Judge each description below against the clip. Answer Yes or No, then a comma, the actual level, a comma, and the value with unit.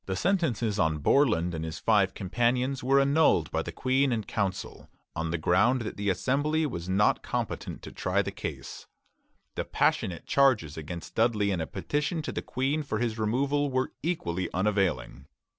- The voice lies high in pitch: No, low, 110 Hz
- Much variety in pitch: Yes, wide, 7.4 semitones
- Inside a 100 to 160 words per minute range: No, average, 175 wpm